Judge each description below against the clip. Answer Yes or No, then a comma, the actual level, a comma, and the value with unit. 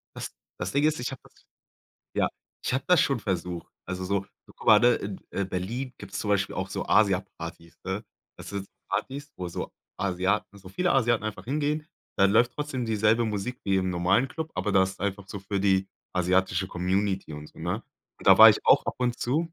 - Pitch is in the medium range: No, low, 100 Hz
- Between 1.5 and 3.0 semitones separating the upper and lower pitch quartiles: No, average, 4.6 semitones